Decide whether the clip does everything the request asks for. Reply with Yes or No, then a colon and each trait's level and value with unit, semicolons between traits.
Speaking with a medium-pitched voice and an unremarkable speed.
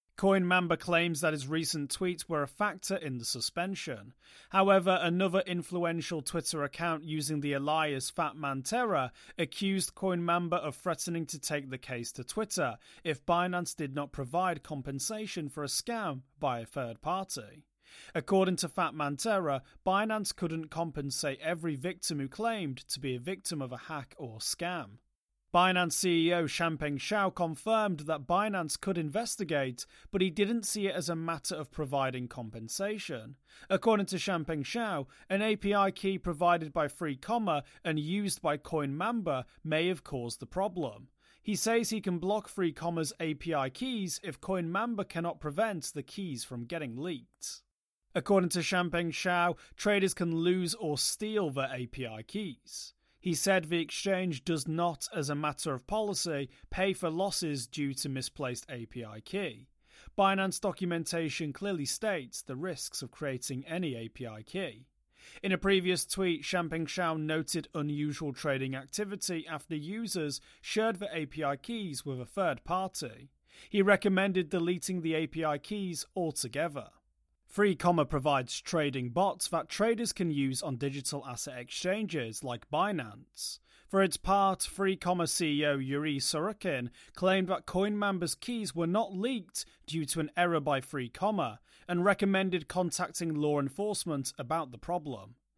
Yes: medium, 165 Hz; average, 145 wpm